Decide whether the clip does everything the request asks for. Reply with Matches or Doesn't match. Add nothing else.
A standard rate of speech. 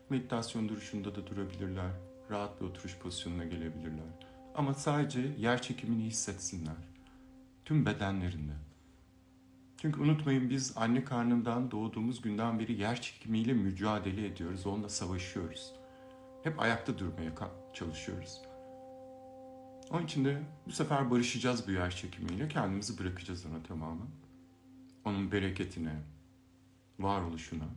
Matches